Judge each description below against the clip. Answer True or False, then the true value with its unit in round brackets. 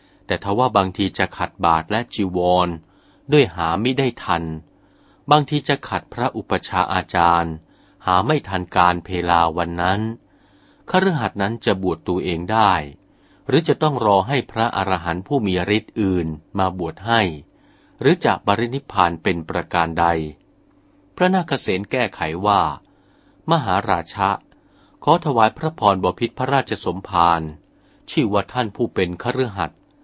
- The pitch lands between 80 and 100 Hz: True (95 Hz)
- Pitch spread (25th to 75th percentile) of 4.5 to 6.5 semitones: True (5.6 semitones)